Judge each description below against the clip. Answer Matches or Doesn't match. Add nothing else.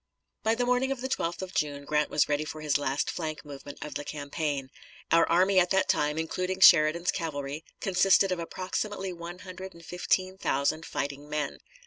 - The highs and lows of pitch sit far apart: Doesn't match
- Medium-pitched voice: Matches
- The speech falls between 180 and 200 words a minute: Matches